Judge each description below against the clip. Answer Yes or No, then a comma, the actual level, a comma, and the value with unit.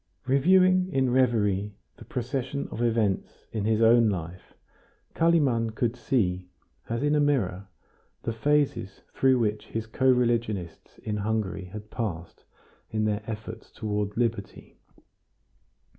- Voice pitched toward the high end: No, low, 115 Hz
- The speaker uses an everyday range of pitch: Yes, average, 3.7 semitones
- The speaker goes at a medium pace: No, slow, 130 wpm